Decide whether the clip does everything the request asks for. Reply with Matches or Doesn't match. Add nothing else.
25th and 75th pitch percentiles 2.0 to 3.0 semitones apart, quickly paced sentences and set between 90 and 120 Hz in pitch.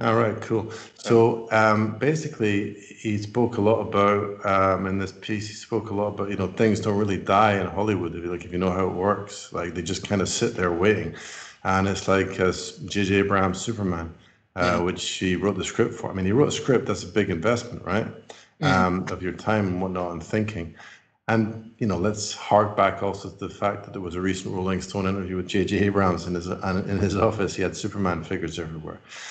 Matches